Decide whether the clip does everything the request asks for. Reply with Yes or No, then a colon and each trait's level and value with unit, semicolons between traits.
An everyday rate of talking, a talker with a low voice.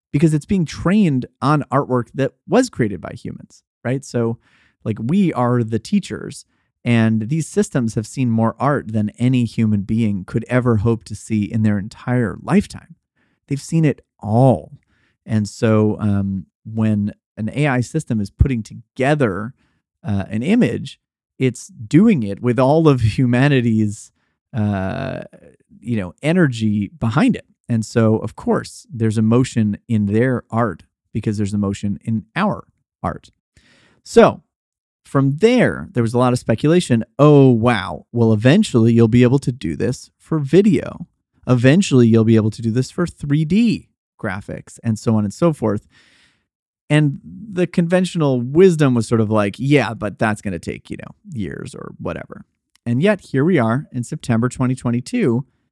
Yes: average, 160 wpm; low, 120 Hz